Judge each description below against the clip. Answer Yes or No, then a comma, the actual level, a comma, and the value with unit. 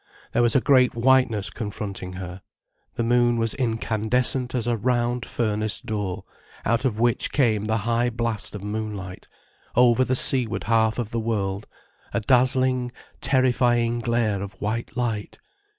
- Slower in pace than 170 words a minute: Yes, average, 150 wpm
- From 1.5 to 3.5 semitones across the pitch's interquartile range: Yes, narrow, 2.4 semitones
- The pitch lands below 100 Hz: No, low, 115 Hz